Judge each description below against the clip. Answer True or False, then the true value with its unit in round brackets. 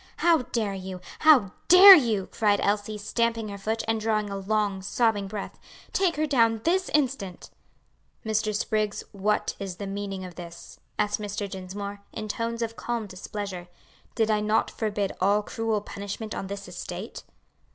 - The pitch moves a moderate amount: False (2.2 semitones)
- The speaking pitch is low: False (210 Hz)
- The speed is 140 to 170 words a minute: True (160 wpm)